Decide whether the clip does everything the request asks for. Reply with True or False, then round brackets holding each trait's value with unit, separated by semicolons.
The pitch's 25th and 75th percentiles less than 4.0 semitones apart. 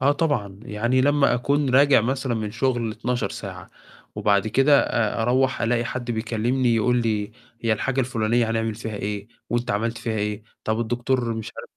True (2.9 semitones)